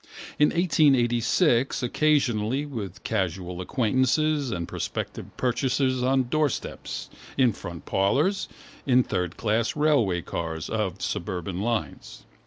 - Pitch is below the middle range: Yes, low, 120 Hz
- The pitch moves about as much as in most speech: No, wide, 6.2 semitones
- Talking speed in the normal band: No, slow, 105 wpm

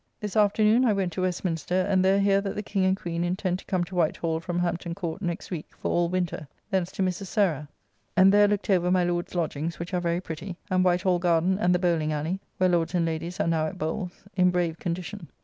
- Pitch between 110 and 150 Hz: No, medium, 180 Hz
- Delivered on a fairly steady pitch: Yes, narrow, 2.0 semitones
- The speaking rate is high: Yes, fast, 240 wpm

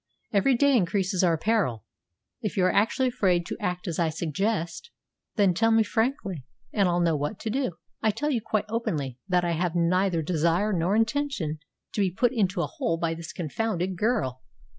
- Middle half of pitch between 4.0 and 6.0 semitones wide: Yes, average, 5.0 semitones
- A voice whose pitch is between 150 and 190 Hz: Yes, medium, 185 Hz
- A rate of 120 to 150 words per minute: No, average, 190 wpm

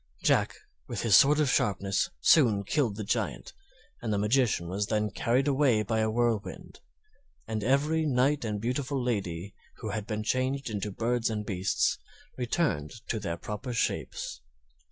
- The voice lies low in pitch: Yes, low, 110 Hz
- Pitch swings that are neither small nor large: Yes, average, 4.0 semitones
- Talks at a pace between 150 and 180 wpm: Yes, average, 155 wpm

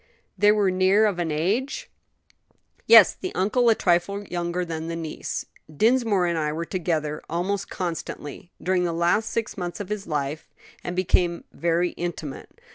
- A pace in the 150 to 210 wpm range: Yes, average, 160 wpm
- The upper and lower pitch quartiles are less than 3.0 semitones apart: No, average, 3.3 semitones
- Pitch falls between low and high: Yes, medium, 175 Hz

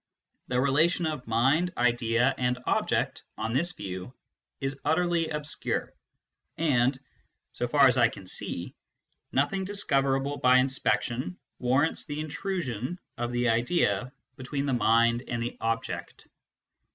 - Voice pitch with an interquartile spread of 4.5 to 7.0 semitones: No, average, 4.0 semitones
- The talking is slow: Yes, slow, 130 wpm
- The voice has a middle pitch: No, low, 130 Hz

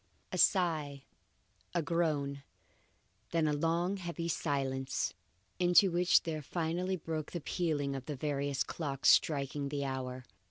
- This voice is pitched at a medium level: Yes, medium, 150 Hz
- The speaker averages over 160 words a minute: No, slow, 135 wpm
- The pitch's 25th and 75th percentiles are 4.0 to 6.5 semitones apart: No, average, 3.5 semitones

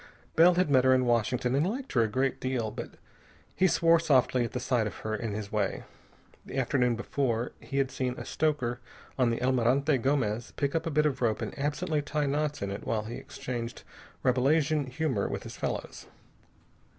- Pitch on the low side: Yes, low, 130 Hz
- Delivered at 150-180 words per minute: No, average, 195 wpm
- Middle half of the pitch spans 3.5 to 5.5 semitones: Yes, average, 3.8 semitones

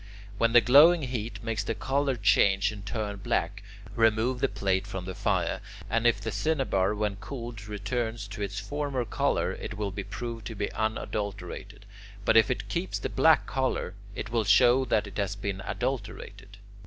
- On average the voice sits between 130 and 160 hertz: No, low, 110 Hz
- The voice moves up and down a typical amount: Yes, average, 3.2 semitones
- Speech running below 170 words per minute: No, average, 180 wpm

